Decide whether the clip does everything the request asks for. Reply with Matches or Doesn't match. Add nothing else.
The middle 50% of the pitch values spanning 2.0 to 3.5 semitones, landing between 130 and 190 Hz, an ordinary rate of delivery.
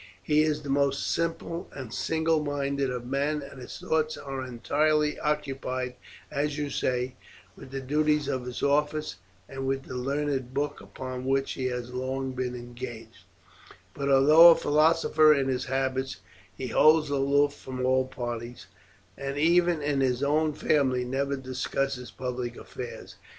Matches